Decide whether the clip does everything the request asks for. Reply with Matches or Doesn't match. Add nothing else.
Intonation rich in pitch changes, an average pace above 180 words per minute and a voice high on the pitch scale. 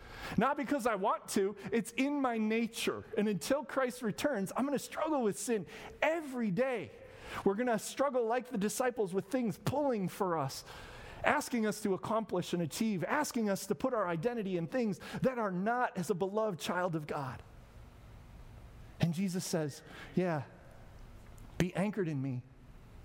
Doesn't match